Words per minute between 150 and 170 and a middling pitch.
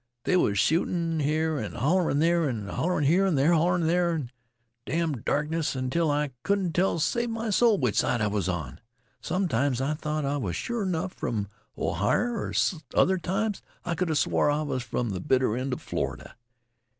No: average, 190 wpm; medium, 155 Hz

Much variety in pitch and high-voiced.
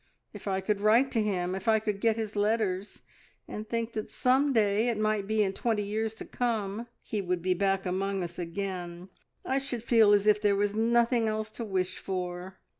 No: narrow, 2.6 semitones; high, 210 Hz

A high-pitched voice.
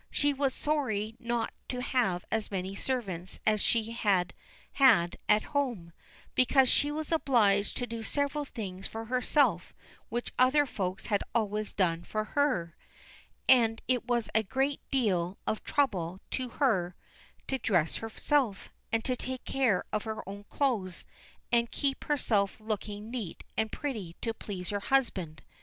Yes: high, 225 Hz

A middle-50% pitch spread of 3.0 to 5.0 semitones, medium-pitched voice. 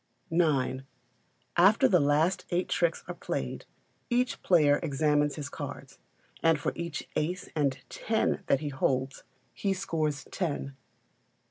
Yes: average, 3.5 semitones; medium, 155 Hz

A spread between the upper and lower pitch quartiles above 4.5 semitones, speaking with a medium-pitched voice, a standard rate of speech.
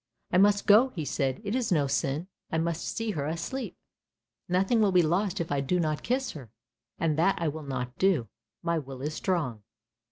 No: average, 5.3 semitones; medium, 165 Hz; fast, 210 wpm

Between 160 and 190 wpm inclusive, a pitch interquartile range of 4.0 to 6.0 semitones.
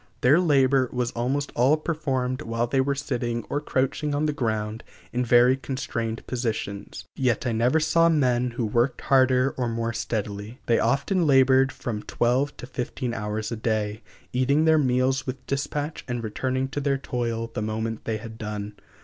No: average, 175 wpm; average, 2.9 semitones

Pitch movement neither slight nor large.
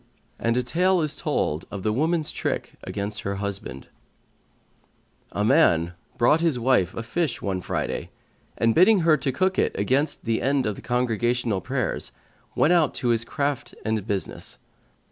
No: wide, 6.5 semitones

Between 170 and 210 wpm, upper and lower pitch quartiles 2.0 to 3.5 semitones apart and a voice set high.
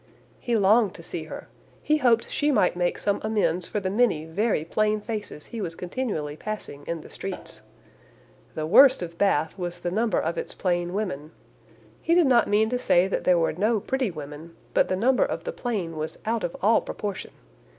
No: average, 200 wpm; average, 5.2 semitones; high, 200 Hz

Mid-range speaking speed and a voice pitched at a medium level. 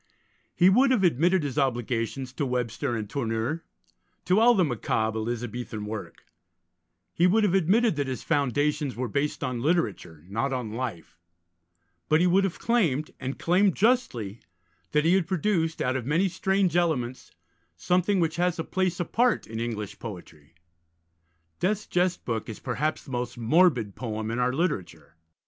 Yes: average, 160 wpm; medium, 145 Hz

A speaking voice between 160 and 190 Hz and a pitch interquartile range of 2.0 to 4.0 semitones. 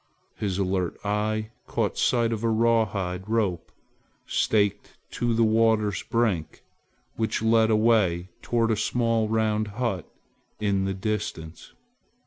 No: low, 110 Hz; narrow, 2.6 semitones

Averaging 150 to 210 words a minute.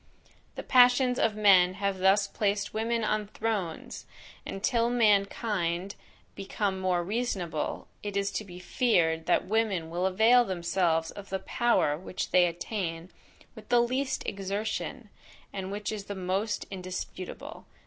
No: average, 140 wpm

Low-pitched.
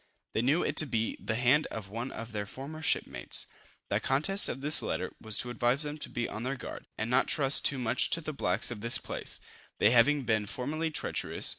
Yes: low, 125 Hz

